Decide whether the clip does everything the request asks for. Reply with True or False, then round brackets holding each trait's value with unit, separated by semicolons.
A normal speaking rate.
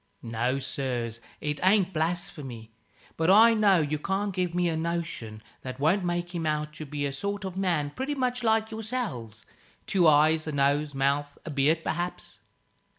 True (170 wpm)